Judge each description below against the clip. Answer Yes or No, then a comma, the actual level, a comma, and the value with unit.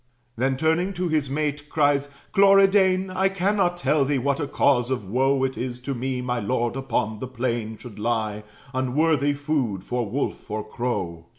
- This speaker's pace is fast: No, average, 175 wpm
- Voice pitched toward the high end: No, low, 135 Hz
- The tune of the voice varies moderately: Yes, average, 4.5 semitones